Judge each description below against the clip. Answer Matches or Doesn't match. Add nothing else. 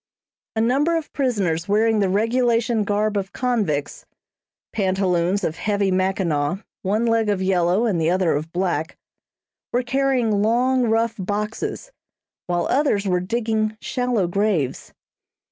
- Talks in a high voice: Matches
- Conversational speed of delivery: Doesn't match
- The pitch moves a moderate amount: Matches